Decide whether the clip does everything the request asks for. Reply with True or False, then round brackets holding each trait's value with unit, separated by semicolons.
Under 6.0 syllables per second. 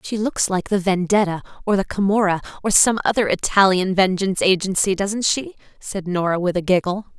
True (5.5 syllables/s)